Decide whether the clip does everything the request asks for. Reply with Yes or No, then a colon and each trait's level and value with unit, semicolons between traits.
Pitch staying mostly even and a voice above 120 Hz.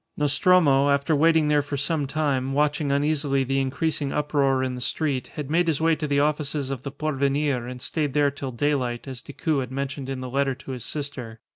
Yes: narrow, 1.9 semitones; medium, 140 Hz